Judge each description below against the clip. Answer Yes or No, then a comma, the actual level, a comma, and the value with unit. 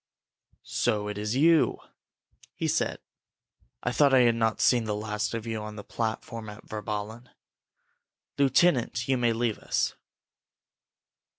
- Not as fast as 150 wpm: Yes, slow, 135 wpm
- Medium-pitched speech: No, low, 115 Hz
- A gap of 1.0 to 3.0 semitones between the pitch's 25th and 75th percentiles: Yes, narrow, 2.4 semitones